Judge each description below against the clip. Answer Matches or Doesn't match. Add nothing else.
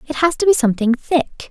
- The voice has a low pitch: Doesn't match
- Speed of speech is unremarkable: Doesn't match